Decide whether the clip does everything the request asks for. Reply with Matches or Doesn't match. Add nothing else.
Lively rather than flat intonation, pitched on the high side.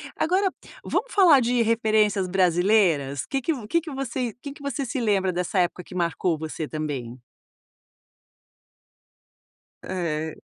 Matches